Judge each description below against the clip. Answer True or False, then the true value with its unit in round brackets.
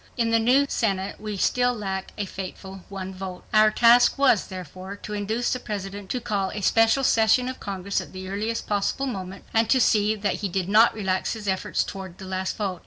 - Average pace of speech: False (210 wpm)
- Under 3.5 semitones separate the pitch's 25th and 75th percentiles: True (2.9 semitones)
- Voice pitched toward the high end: True (205 Hz)